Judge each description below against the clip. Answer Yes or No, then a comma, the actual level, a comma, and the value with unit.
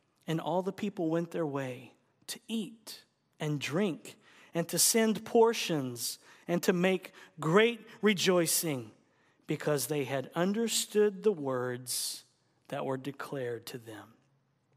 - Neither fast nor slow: No, slow, 125 wpm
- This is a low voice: No, medium, 165 Hz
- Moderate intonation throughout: No, wide, 7.1 semitones